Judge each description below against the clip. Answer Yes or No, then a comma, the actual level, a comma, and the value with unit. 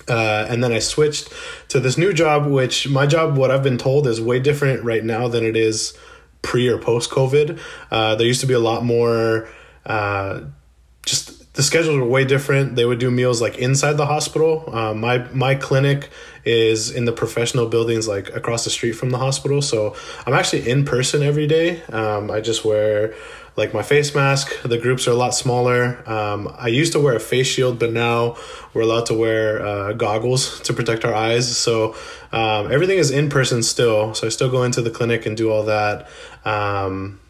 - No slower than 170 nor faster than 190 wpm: No, fast, 205 wpm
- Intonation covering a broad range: No, average, 3.5 semitones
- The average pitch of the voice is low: Yes, low, 120 Hz